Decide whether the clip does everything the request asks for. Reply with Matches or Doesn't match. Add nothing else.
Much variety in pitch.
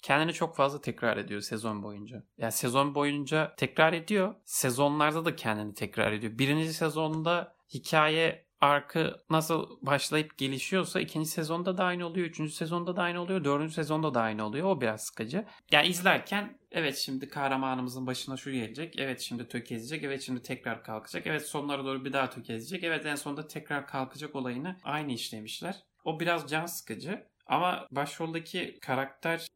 Doesn't match